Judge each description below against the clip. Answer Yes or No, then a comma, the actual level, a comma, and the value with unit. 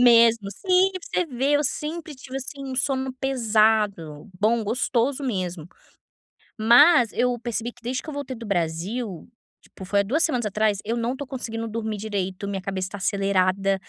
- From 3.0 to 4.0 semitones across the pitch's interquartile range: No, average, 4.8 semitones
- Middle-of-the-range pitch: No, high, 230 Hz